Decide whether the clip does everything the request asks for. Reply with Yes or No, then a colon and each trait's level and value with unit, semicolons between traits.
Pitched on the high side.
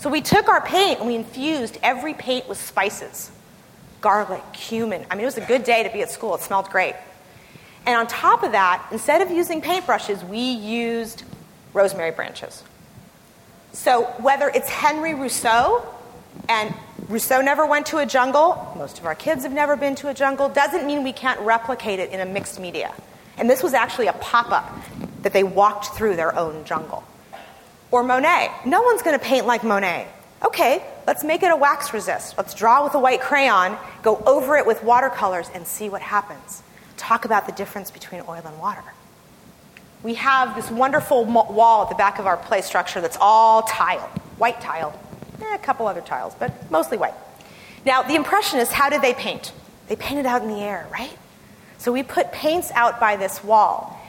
Yes: high, 235 Hz